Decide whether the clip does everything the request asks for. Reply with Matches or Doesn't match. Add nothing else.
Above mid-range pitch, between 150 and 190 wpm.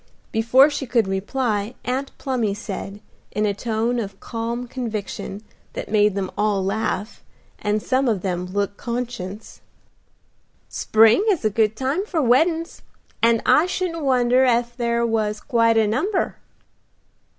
Doesn't match